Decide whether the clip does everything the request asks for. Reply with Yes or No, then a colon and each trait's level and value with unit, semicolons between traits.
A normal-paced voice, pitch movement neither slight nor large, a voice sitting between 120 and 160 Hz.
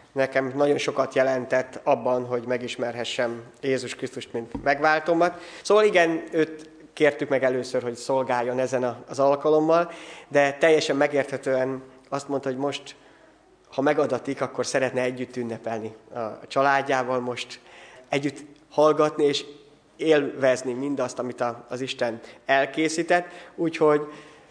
Yes: average, 120 wpm; average, 3.2 semitones; low, 135 Hz